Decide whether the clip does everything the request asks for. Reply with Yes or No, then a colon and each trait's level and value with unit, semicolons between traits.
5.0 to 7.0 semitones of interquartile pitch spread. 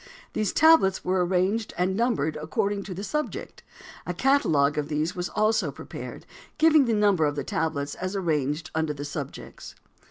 Yes: wide, 5.6 semitones